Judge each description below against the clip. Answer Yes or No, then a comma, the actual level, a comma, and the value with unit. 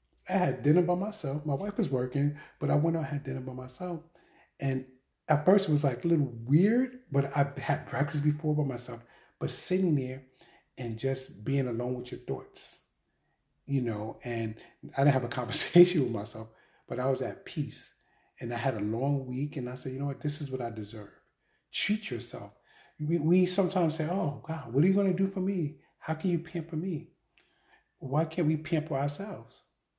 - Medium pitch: Yes, medium, 145 Hz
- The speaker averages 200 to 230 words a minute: Yes, fast, 205 wpm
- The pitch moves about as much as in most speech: Yes, average, 4.5 semitones